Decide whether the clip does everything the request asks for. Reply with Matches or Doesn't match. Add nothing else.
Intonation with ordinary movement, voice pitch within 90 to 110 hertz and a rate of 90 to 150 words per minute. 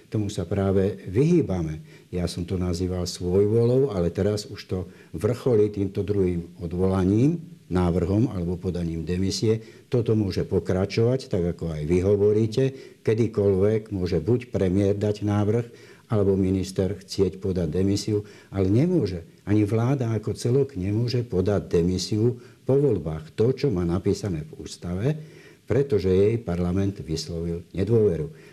Matches